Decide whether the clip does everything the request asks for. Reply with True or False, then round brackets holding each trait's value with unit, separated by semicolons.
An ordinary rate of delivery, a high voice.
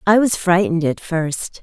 False (185 wpm; 180 Hz)